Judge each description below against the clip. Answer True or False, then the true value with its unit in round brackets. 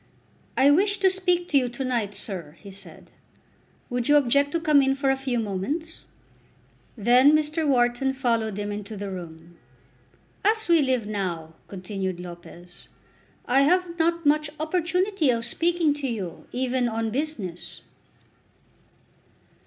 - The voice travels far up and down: True (7.0 semitones)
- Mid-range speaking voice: False (255 Hz)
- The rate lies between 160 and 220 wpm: False (145 wpm)